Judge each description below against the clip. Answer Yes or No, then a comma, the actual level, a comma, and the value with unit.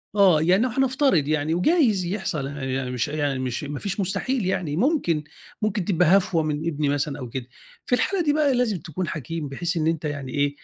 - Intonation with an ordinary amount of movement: No, wide, 5.8 semitones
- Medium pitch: Yes, medium, 165 Hz